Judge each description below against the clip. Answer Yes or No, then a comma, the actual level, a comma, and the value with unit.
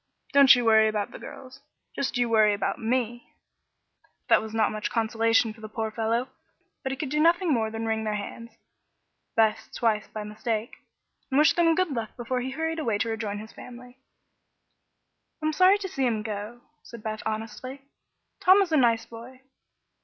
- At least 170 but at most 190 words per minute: Yes, average, 185 wpm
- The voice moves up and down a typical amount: Yes, average, 3.3 semitones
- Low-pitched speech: No, high, 230 Hz